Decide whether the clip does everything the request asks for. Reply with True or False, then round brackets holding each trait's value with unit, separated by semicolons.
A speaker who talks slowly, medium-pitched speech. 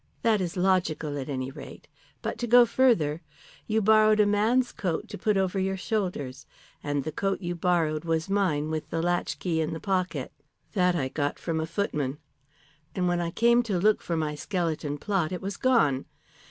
False (190 wpm; 175 Hz)